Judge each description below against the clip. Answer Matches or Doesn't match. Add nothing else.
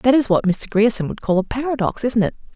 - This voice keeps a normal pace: Doesn't match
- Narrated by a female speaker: Matches